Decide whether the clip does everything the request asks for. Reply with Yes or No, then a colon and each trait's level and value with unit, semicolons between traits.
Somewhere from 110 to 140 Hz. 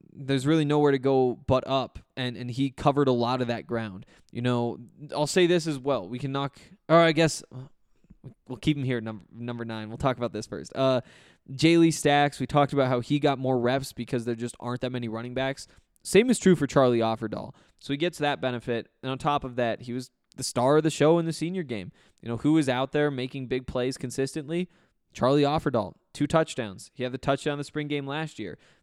Yes: low, 135 Hz